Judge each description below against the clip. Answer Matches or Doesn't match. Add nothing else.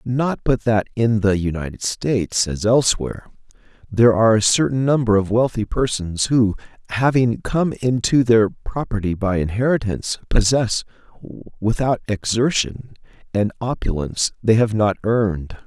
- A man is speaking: Matches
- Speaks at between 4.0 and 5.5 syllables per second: Matches